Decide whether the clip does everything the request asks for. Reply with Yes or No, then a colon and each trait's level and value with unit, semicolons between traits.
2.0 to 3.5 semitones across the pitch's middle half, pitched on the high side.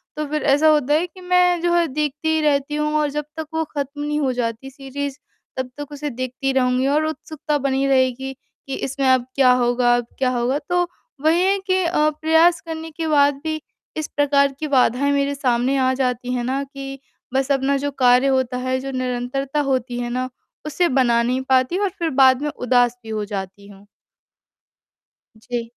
Yes: average, 3.0 semitones; very high, 275 Hz